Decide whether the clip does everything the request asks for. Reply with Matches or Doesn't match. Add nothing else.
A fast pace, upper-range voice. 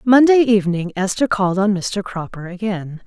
Doesn't match